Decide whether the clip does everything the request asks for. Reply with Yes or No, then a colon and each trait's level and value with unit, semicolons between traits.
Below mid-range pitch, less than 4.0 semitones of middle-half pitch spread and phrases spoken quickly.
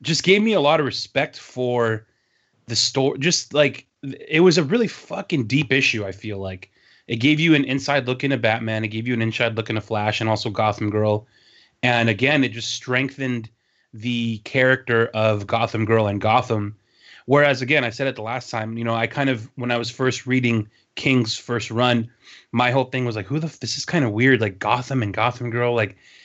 Yes: low, 120 Hz; average, 3.4 semitones; fast, 220 wpm